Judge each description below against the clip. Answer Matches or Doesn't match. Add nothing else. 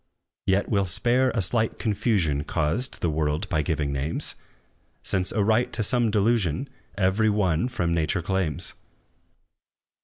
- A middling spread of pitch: Doesn't match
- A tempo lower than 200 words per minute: Matches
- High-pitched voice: Doesn't match